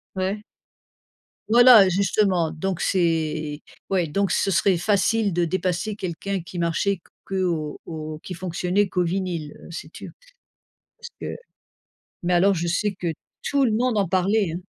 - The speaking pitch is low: No, medium, 185 Hz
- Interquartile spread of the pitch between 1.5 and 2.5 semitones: No, average, 2.9 semitones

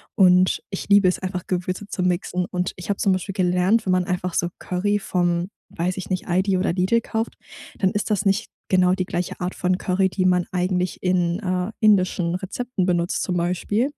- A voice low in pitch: No, medium, 185 Hz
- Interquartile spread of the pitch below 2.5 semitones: Yes, narrow, 1.4 semitones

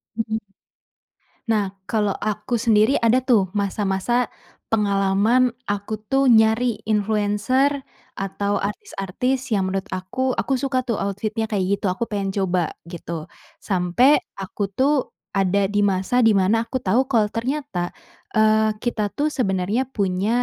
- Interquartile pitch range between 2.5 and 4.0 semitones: Yes, average, 3.2 semitones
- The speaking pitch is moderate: No, high, 210 Hz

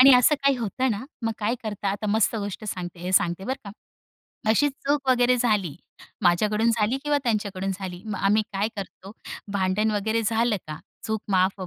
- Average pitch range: Yes, average, 3.5 semitones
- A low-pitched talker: No, high, 215 Hz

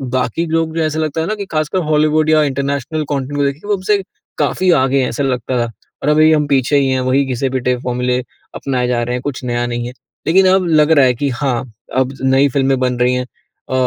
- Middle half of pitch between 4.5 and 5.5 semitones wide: No, average, 3.5 semitones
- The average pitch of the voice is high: No, medium, 140 Hz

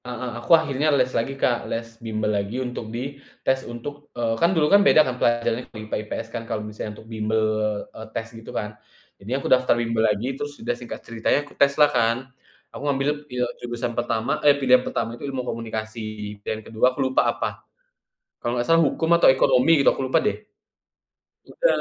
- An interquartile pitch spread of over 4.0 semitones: No, average, 2.8 semitones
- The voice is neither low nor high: No, low, 120 Hz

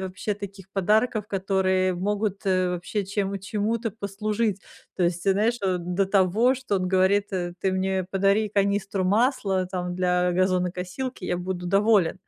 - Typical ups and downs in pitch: No, narrow, 2.0 semitones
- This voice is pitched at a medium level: No, high, 195 Hz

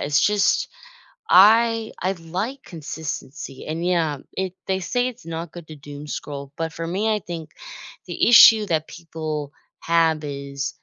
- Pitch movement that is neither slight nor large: Yes, average, 4.1 semitones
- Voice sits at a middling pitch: Yes, medium, 165 Hz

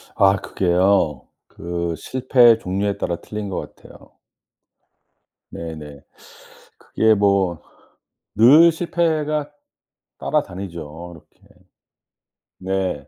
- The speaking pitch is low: Yes, very low, 95 Hz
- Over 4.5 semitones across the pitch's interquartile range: Yes, wide, 5.4 semitones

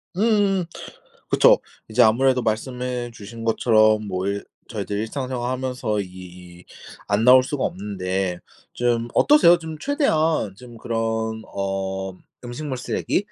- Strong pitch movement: No, average, 4.3 semitones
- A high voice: No, low, 115 Hz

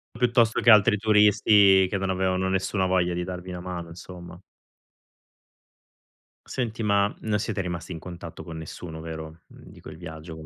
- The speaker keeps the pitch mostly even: No, average, 3.1 semitones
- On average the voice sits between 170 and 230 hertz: No, very low, 95 Hz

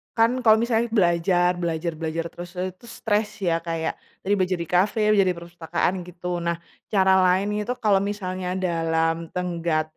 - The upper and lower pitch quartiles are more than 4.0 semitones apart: No, narrow, 2.5 semitones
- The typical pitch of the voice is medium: Yes, medium, 180 Hz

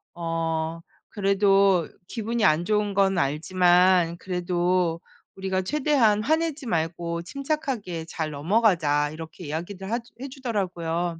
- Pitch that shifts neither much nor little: Yes, average, 4.2 semitones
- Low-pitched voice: No, medium, 185 Hz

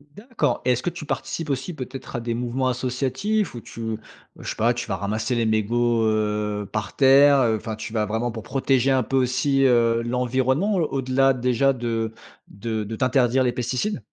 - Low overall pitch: Yes, low, 125 Hz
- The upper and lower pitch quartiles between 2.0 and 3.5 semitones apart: Yes, average, 3.0 semitones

